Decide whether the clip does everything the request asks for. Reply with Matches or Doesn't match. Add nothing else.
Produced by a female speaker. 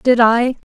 Matches